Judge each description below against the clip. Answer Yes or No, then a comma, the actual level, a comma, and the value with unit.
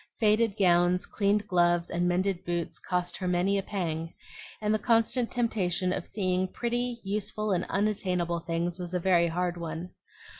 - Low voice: No, medium, 185 Hz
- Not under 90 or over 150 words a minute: No, average, 160 wpm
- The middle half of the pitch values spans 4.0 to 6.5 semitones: No, average, 3.2 semitones